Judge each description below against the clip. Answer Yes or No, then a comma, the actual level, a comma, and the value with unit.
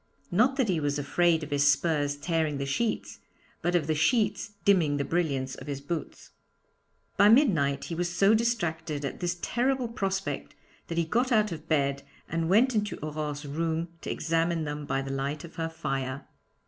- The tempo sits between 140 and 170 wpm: No, average, 185 wpm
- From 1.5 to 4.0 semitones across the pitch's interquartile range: No, average, 5.0 semitones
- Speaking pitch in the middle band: Yes, medium, 165 Hz